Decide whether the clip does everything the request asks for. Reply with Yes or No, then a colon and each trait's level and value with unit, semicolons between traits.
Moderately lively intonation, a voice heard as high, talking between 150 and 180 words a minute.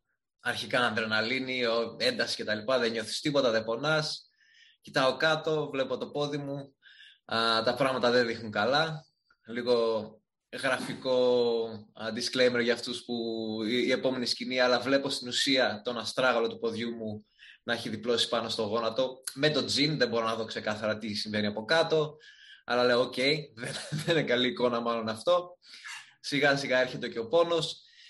No: average, 4.0 semitones; low, 125 Hz; average, 160 wpm